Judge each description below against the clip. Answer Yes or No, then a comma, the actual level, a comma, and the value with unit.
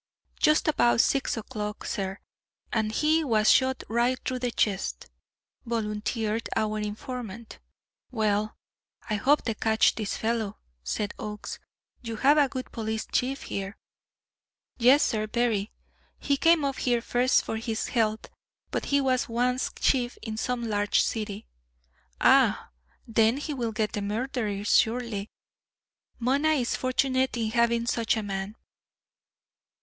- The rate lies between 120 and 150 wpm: Yes, slow, 135 wpm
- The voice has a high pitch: Yes, high, 230 Hz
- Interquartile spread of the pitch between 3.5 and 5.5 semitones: No, average, 3.0 semitones